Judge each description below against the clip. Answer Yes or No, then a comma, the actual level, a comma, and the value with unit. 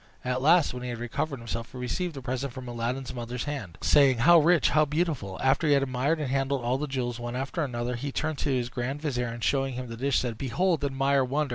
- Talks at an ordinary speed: No, fast, 245 wpm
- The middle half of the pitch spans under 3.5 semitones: Yes, average, 2.9 semitones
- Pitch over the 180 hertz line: No, low, 130 Hz